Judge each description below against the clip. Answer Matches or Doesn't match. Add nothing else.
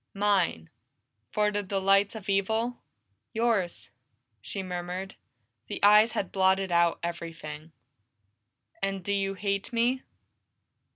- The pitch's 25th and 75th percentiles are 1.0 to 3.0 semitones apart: Matches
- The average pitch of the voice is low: Doesn't match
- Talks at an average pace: Doesn't match